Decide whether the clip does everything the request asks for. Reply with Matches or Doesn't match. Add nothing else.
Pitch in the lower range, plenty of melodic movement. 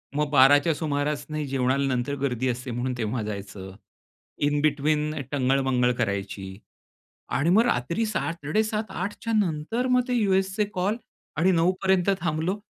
Doesn't match